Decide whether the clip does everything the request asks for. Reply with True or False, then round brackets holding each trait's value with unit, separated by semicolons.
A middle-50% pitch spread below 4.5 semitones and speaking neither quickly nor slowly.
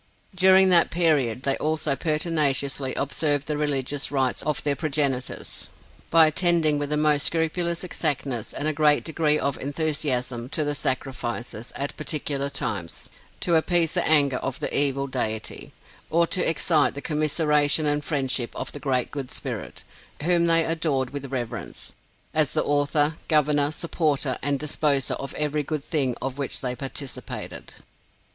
True (2.4 semitones; 150 wpm)